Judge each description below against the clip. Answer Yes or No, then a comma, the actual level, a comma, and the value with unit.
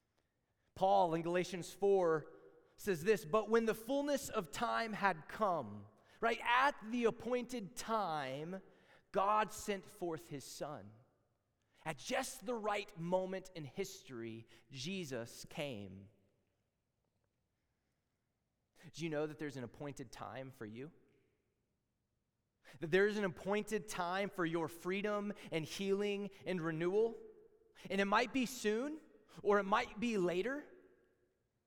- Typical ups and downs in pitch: No, wide, 8.2 semitones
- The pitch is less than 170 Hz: No, medium, 185 Hz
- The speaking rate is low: Yes, slow, 125 wpm